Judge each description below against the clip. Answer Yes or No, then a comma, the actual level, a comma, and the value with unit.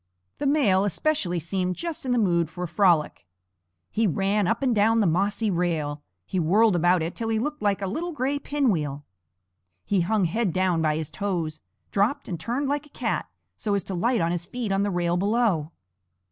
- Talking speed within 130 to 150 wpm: No, average, 200 wpm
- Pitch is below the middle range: No, high, 195 Hz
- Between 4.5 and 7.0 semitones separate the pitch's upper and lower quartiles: Yes, average, 4.9 semitones